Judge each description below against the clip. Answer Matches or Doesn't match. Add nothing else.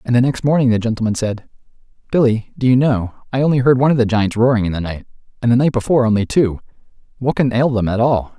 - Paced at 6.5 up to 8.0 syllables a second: Matches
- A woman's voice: Doesn't match